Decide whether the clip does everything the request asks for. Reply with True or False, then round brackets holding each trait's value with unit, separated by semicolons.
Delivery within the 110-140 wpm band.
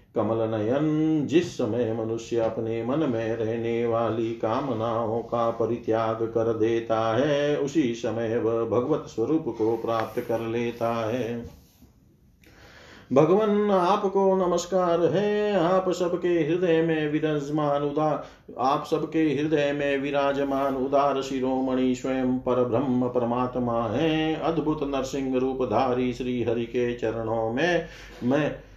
True (125 wpm)